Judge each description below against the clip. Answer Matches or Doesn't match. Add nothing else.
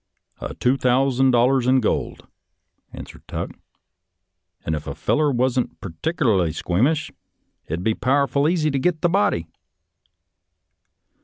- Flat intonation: Doesn't match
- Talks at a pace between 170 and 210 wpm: Doesn't match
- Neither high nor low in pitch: Doesn't match